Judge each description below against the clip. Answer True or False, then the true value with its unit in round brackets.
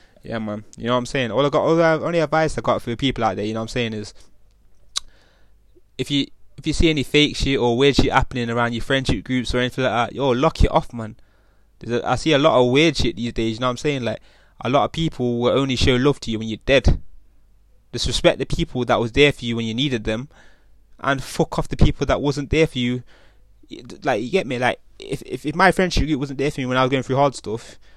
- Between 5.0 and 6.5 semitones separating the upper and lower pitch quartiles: False (4.1 semitones)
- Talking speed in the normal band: False (270 wpm)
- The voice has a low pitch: True (125 Hz)